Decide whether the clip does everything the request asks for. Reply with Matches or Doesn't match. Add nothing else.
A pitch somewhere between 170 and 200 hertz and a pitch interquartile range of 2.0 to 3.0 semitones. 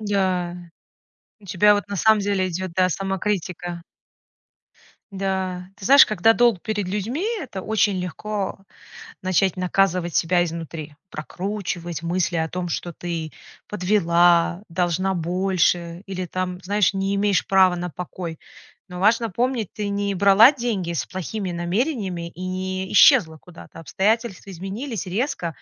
Matches